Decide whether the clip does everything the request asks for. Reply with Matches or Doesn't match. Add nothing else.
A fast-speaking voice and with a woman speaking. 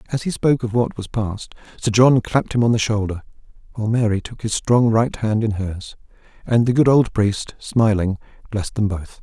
Doesn't match